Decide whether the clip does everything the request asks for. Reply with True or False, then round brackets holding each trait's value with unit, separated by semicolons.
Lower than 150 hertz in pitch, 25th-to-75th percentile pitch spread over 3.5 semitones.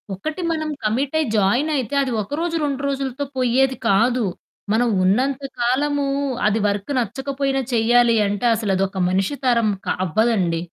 False (245 Hz; 4.6 semitones)